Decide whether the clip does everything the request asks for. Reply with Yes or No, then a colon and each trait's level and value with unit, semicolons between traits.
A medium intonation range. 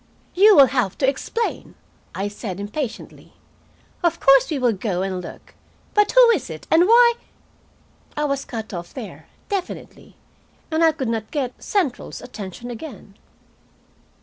No: wide, 7.6 semitones